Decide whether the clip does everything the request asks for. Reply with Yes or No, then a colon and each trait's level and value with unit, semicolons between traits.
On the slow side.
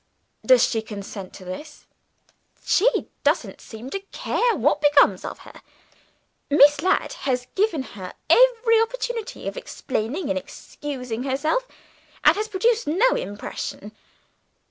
Yes: slow, 125 wpm